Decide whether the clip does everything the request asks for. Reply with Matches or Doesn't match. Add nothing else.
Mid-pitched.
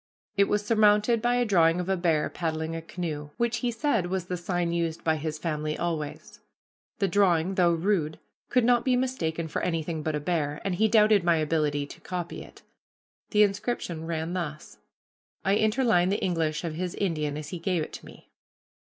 Matches